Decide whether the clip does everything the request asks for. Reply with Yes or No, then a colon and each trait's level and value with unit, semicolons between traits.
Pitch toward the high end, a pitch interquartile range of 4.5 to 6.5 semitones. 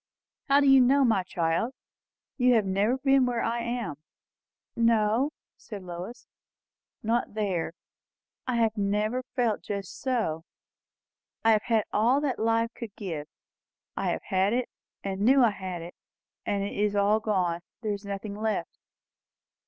No: high, 215 Hz; average, 3.4 semitones